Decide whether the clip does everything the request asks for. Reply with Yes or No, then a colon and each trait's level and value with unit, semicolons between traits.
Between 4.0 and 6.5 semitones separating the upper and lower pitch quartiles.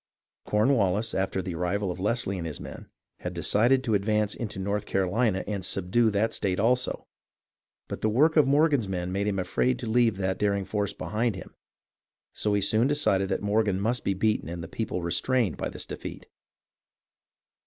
No: average, 3.4 semitones